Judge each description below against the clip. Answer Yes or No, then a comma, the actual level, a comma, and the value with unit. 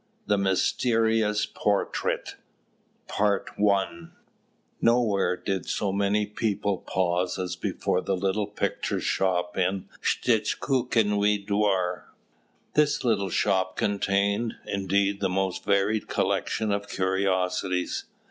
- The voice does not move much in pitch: Yes, narrow, 1.8 semitones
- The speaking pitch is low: Yes, low, 100 Hz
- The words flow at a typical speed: No, slow, 105 wpm